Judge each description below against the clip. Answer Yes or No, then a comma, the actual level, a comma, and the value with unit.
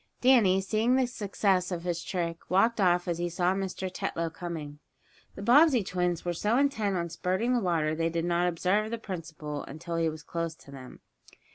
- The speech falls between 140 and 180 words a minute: No, average, 200 wpm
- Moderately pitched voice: Yes, medium, 180 Hz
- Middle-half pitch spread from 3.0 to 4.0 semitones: Yes, average, 3.5 semitones